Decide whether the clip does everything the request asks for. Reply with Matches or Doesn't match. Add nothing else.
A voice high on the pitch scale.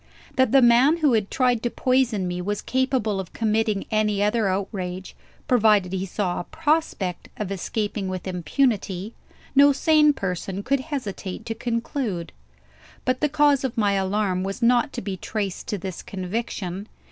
Matches